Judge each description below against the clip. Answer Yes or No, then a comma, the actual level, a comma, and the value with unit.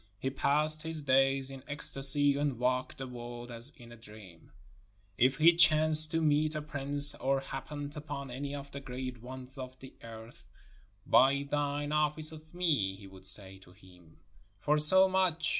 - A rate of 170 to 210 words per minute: Yes, average, 175 wpm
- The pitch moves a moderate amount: Yes, average, 3.6 semitones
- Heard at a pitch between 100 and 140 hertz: Yes, low, 135 Hz